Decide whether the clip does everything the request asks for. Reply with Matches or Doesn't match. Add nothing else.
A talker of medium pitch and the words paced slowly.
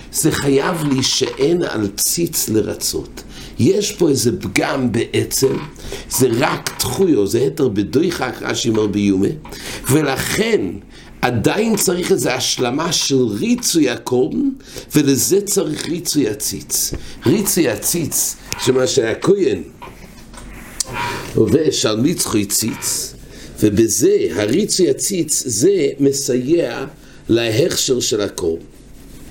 Matches